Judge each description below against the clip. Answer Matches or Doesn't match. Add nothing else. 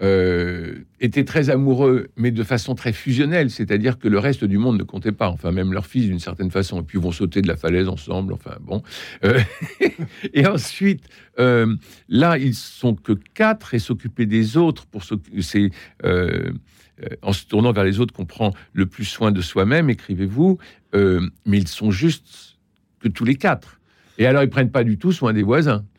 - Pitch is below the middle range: Matches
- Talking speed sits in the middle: Matches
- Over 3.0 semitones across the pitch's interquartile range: Matches